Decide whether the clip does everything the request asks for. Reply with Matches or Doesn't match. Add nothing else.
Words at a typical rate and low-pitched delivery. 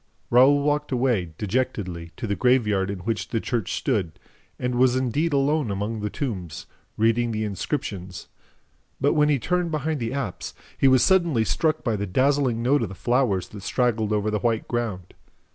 Matches